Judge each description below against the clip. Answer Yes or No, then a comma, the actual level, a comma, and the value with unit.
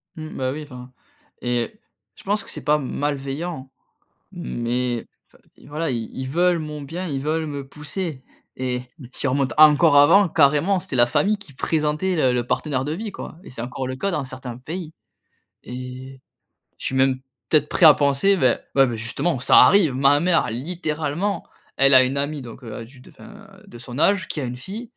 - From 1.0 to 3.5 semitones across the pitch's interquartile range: No, average, 4.3 semitones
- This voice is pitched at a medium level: Yes, medium, 145 Hz